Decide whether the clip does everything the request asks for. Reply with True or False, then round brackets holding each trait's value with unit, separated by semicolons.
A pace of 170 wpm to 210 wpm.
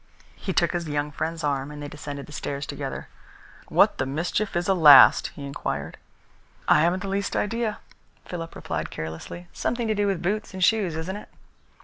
True (190 wpm)